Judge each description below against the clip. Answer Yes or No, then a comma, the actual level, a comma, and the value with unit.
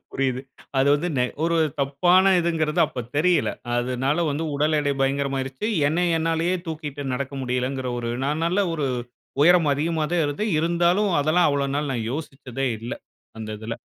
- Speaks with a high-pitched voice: No, medium, 145 Hz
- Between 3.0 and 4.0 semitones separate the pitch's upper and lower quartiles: Yes, average, 3.7 semitones